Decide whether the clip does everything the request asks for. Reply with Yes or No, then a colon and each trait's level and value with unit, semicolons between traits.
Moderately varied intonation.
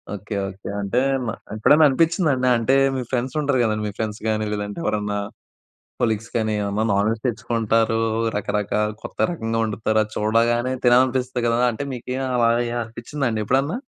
Yes: average, 3.0 semitones